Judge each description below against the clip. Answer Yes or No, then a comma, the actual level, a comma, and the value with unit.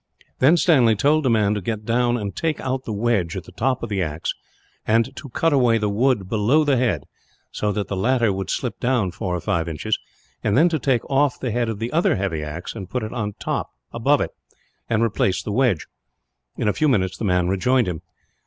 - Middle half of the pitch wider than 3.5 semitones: Yes, average, 4.7 semitones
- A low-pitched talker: Yes, low, 115 Hz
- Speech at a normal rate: No, fast, 220 wpm